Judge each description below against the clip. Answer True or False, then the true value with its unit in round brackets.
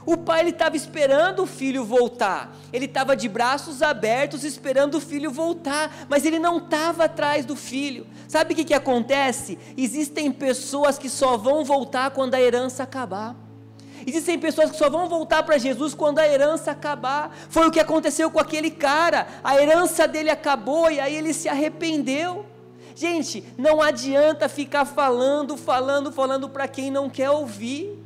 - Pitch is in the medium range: False (290 Hz)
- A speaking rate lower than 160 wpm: False (165 wpm)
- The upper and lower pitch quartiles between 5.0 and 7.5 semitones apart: False (2.7 semitones)